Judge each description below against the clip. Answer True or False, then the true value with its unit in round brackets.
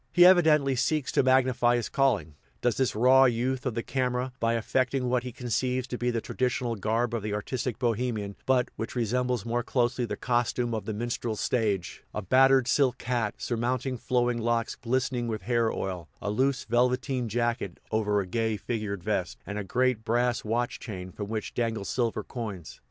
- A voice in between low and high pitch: False (120 Hz)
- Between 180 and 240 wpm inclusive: True (185 wpm)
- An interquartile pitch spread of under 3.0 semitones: True (2.4 semitones)